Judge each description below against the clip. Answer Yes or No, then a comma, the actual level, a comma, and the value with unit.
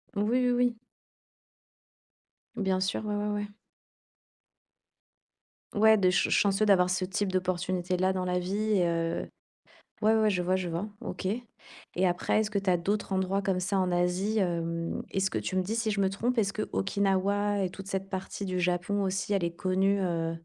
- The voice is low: No, high, 190 Hz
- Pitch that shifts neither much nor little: No, narrow, 2.1 semitones